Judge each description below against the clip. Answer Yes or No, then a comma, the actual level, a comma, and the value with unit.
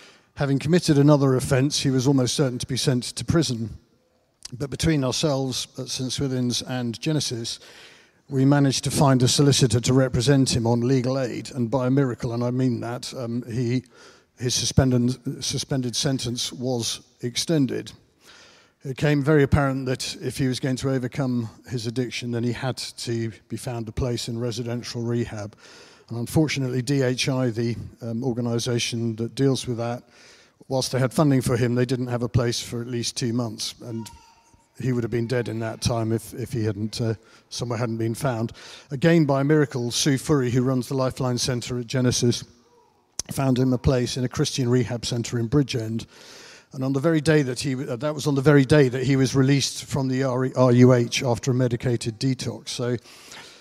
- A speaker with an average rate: Yes, average, 185 wpm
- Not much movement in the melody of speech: Yes, narrow, 2.3 semitones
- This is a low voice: Yes, low, 125 Hz